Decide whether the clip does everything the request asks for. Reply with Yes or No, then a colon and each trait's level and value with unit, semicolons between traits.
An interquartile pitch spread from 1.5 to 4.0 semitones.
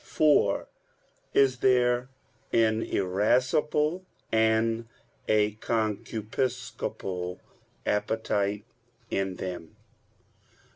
Yes: average, 3.3 semitones